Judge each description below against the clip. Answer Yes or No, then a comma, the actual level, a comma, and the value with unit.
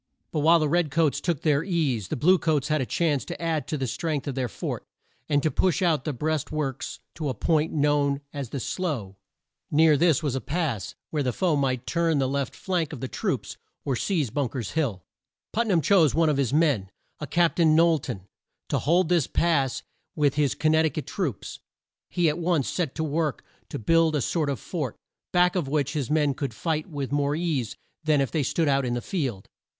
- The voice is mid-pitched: Yes, medium, 150 Hz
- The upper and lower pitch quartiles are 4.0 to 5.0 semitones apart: No, average, 3.3 semitones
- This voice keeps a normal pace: No, fast, 220 wpm